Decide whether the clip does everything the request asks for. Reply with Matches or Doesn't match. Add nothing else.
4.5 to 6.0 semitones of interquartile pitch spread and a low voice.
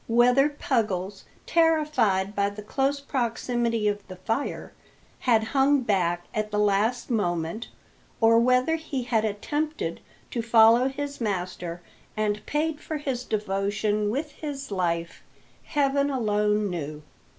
Doesn't match